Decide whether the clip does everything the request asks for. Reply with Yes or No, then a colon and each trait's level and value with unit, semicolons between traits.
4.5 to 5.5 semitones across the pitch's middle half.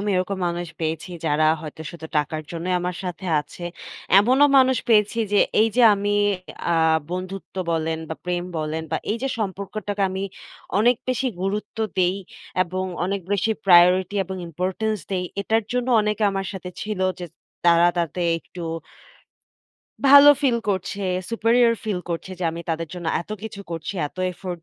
No: average, 3.6 semitones